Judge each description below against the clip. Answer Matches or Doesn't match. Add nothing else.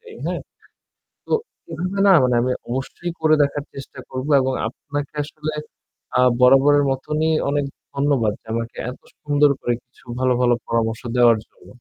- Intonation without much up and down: Doesn't match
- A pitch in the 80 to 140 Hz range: Matches